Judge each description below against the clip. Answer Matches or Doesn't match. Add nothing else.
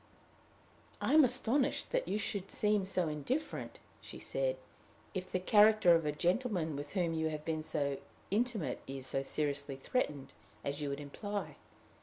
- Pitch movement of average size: Doesn't match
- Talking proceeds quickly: Doesn't match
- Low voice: Doesn't match